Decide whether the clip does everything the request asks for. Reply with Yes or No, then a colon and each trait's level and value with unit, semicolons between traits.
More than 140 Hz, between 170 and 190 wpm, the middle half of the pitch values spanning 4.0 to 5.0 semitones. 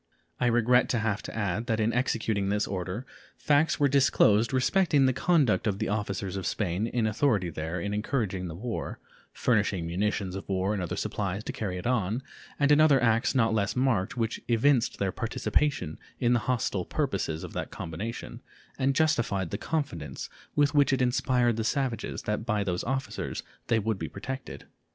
No: low, 110 Hz; average, 185 wpm; average, 4.6 semitones